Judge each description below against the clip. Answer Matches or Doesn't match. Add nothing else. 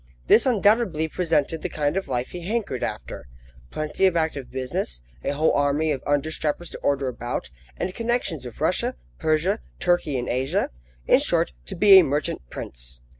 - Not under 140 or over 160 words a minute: Doesn't match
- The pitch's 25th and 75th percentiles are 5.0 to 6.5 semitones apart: Matches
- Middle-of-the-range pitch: Matches